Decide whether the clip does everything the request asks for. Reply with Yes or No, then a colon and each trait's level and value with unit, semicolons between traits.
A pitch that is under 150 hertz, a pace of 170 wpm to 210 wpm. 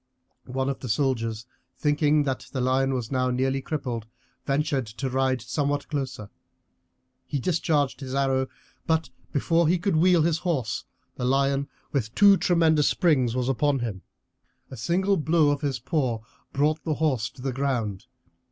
No: low, 135 Hz; average, 160 wpm